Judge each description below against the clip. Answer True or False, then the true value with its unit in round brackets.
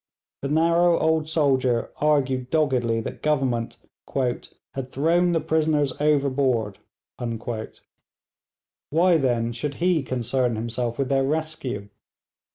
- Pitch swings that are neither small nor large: True (4.3 semitones)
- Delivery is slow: True (105 wpm)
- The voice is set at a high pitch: False (135 Hz)